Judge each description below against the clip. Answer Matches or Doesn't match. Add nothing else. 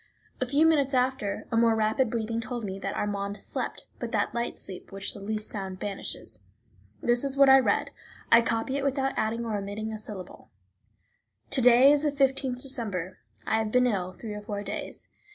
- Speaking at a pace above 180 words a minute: Matches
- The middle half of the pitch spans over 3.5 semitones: Matches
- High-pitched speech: Matches